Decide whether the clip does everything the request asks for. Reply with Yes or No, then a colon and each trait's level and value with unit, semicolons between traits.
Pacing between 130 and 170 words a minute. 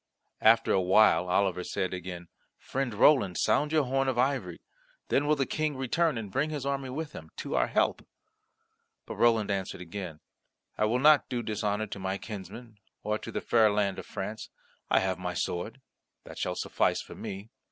No: average, 185 wpm